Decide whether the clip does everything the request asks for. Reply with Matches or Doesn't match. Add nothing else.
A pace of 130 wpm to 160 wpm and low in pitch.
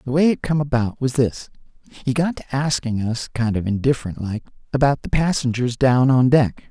Doesn't match